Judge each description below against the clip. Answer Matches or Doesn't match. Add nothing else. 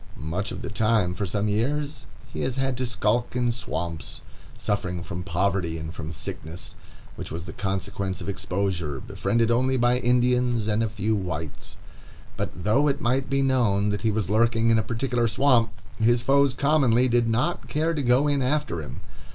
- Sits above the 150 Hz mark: Doesn't match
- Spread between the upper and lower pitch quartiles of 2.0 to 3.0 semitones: Doesn't match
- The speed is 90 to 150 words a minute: Doesn't match